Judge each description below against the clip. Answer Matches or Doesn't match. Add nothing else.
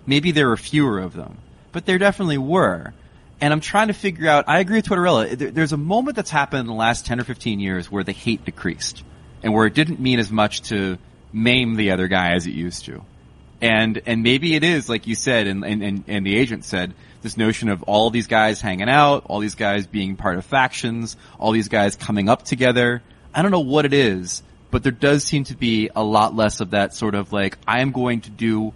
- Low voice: Matches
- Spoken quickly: Matches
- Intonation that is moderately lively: Doesn't match